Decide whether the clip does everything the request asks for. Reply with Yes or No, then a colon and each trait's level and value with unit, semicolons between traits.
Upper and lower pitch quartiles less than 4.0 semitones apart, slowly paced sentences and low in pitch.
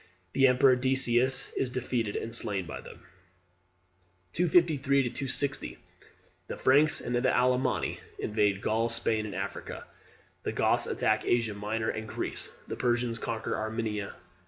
Yes: average, 3.1 semitones; slow, 130 wpm; low, 120 Hz